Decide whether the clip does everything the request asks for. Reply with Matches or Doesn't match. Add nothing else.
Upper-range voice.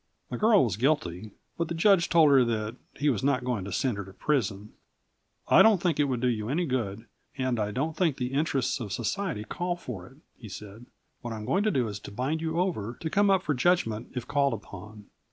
Doesn't match